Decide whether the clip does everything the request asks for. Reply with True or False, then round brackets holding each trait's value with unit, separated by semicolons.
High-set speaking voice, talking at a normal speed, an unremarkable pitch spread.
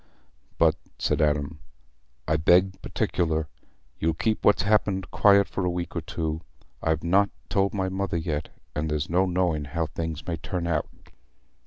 False (85 Hz; 160 wpm; 3.3 semitones)